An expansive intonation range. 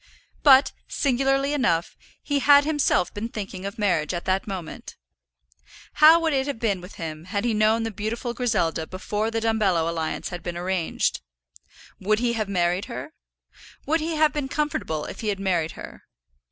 Yes: wide, 6.8 semitones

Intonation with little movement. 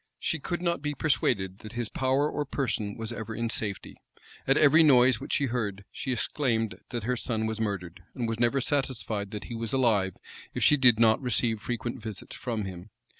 No: average, 3.5 semitones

